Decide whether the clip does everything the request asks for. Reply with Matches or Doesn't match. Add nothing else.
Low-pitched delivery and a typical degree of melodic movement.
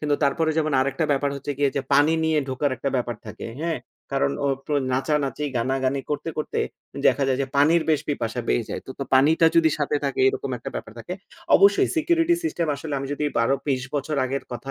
Doesn't match